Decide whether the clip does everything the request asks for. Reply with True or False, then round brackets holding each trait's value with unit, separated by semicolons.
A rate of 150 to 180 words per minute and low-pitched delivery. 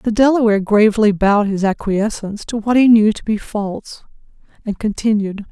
False (165 wpm; 215 Hz)